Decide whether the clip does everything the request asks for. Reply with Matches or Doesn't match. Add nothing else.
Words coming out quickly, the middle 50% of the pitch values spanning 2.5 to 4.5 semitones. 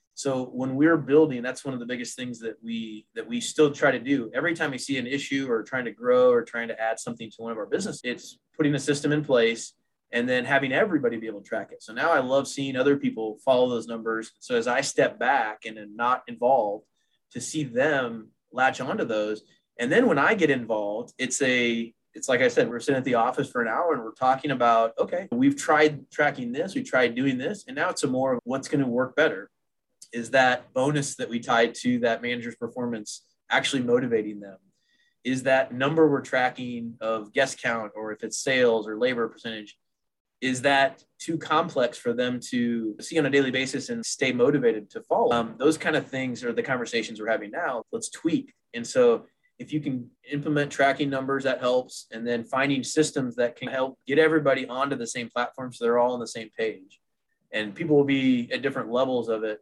Matches